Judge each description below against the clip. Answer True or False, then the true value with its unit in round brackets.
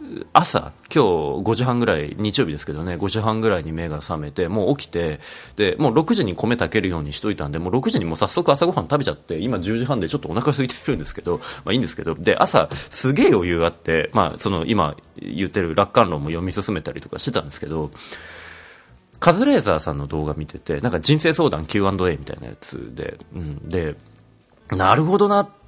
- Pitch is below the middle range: True (100 Hz)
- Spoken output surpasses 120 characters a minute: True (405 characters per minute)